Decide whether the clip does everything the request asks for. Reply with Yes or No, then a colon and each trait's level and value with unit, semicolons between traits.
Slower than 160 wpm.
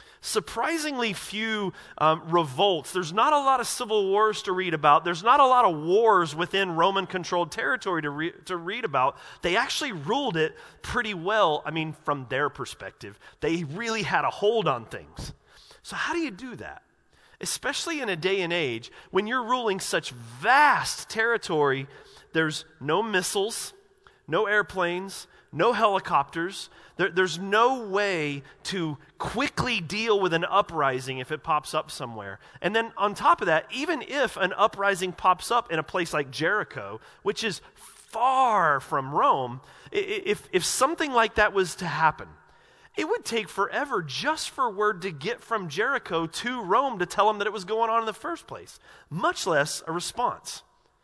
No: average, 170 wpm